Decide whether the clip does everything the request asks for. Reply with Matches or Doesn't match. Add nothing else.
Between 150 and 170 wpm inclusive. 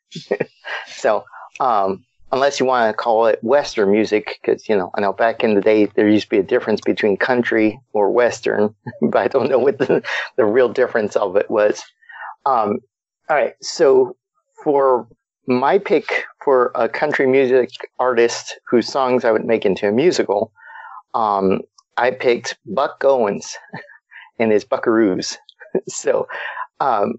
Matches